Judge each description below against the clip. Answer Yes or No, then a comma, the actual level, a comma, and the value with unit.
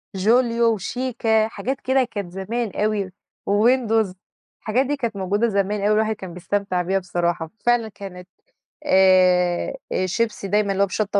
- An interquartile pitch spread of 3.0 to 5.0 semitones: Yes, average, 3.4 semitones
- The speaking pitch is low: No, high, 205 Hz